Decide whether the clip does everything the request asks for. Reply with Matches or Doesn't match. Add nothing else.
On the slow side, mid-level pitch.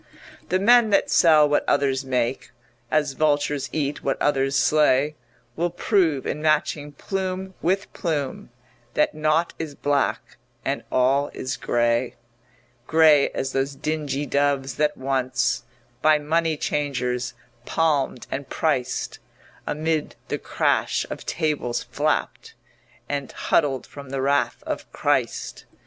Matches